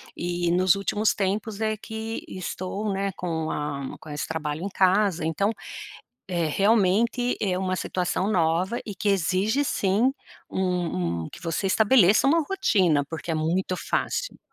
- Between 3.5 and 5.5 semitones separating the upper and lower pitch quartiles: Yes, average, 3.9 semitones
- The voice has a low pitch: No, medium, 185 Hz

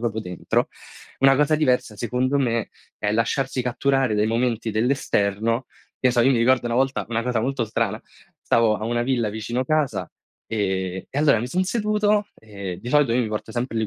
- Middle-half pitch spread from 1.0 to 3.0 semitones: No, average, 3.4 semitones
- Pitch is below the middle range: Yes, low, 120 Hz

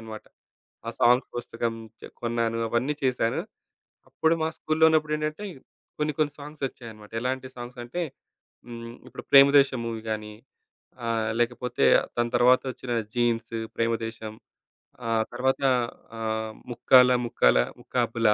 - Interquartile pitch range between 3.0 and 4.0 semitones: No, narrow, 2.6 semitones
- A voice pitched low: Yes, low, 120 Hz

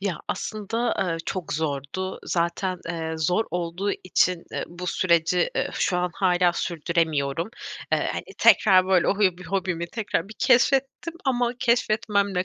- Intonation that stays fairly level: No, average, 3.1 semitones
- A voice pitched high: No, medium, 180 Hz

